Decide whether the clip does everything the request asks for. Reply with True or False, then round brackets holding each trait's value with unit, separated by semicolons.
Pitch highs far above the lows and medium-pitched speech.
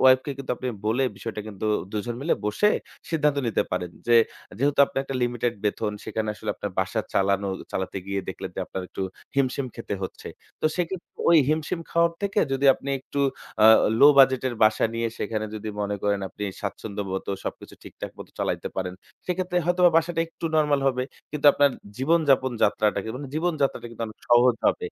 False (6.0 semitones; 125 Hz)